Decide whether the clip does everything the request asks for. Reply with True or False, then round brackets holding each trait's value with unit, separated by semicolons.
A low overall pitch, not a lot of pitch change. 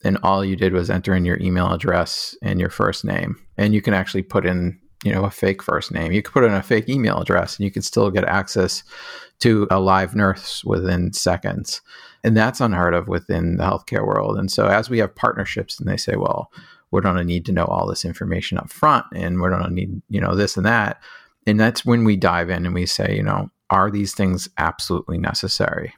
True (95 Hz; 2.3 semitones)